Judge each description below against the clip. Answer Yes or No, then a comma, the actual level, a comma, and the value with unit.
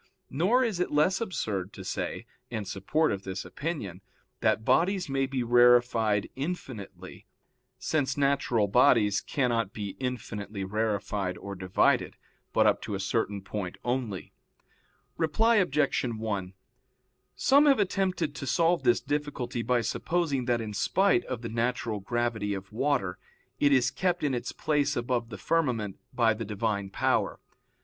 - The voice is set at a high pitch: No, low, 120 Hz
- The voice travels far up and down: Yes, wide, 6.0 semitones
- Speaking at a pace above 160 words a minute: No, average, 145 wpm